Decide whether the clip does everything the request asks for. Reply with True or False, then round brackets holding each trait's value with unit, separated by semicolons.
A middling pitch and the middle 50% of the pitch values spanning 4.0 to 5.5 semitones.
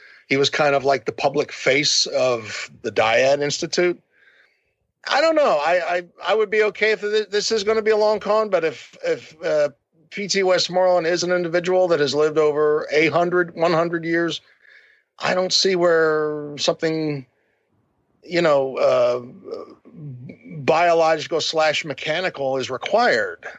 True (170 Hz; 5.0 semitones)